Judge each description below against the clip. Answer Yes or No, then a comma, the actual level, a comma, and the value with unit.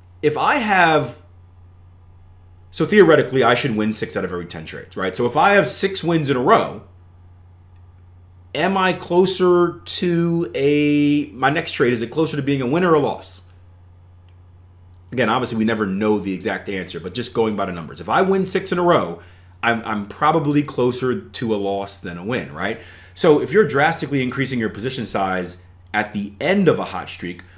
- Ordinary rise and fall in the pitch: No, wide, 8.5 semitones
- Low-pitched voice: Yes, low, 105 Hz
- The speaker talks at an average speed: Yes, average, 195 wpm